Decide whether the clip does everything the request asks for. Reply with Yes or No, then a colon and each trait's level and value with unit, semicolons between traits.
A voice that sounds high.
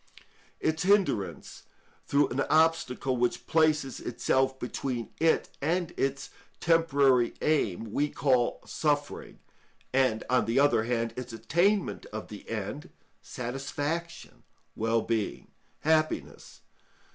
No: low, 135 Hz